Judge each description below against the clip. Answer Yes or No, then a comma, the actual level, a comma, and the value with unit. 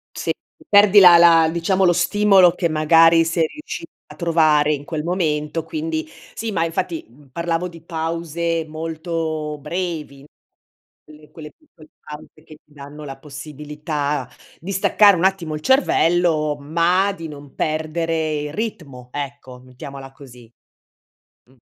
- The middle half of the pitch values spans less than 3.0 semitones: Yes, narrow, 2.6 semitones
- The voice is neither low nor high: Yes, medium, 160 Hz